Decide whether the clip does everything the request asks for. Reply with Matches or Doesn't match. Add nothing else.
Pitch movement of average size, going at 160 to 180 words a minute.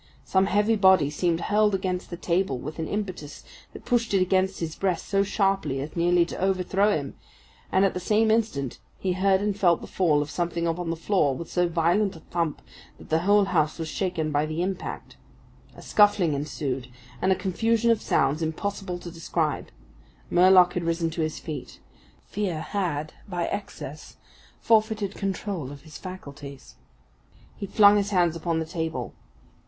Matches